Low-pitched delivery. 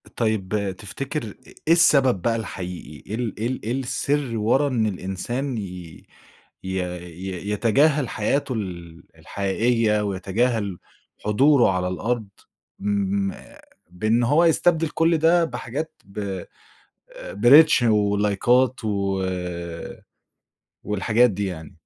Yes: low, 110 Hz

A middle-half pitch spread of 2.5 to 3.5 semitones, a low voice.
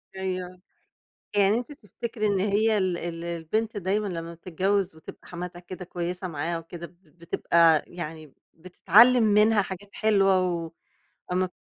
No: average, 3.2 semitones; medium, 185 Hz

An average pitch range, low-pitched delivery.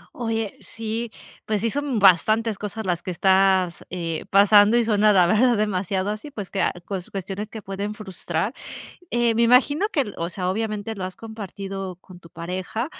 No: average, 3.1 semitones; high, 205 Hz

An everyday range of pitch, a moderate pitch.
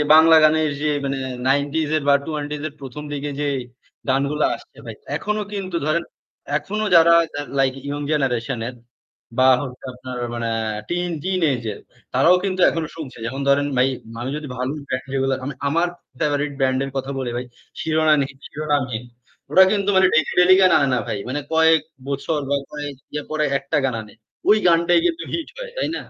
Yes: average, 3.3 semitones; medium, 145 Hz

